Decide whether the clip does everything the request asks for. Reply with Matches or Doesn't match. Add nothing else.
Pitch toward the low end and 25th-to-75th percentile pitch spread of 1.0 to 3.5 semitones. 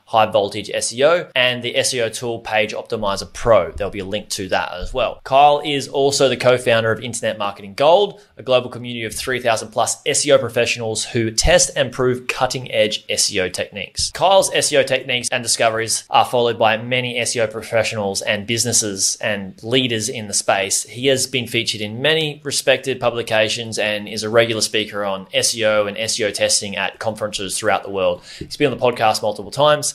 Matches